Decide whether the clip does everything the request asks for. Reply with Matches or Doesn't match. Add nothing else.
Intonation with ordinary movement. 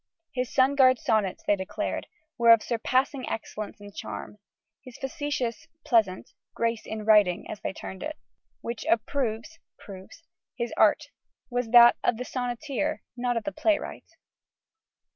Matches